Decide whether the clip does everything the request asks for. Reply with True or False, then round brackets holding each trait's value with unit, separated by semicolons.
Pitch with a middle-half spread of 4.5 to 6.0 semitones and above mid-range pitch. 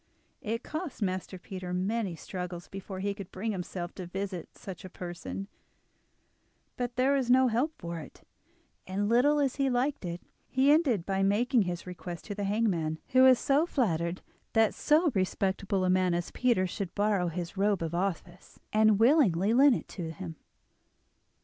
True (5.2 semitones; 195 Hz)